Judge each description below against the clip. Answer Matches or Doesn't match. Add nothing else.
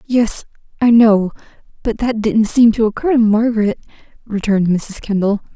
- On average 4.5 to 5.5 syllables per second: Matches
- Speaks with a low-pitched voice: Doesn't match